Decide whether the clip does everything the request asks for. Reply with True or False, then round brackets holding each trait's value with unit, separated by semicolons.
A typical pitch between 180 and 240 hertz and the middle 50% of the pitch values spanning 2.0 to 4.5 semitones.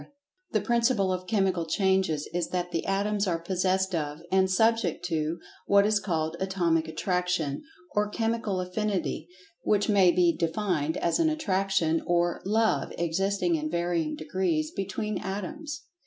True (185 Hz; 3.3 semitones)